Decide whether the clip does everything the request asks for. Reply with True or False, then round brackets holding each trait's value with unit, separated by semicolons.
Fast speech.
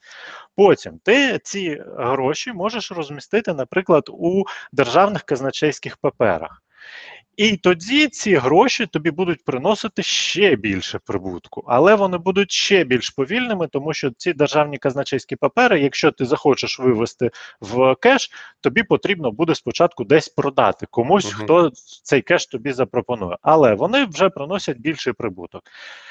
False (130 wpm)